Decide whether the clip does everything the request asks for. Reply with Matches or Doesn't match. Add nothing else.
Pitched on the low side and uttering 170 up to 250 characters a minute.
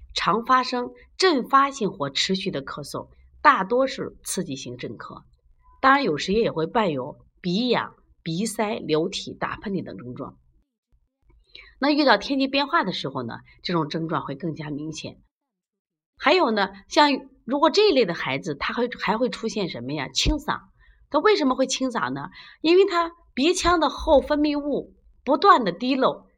Doesn't match